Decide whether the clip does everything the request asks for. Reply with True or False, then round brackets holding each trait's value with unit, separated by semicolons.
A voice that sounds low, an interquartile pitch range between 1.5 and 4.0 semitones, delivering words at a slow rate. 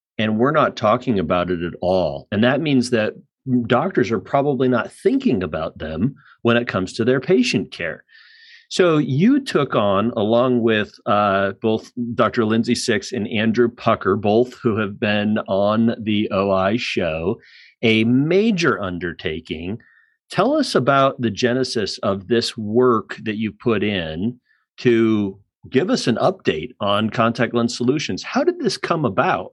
False (120 Hz; 3.5 semitones; 155 wpm)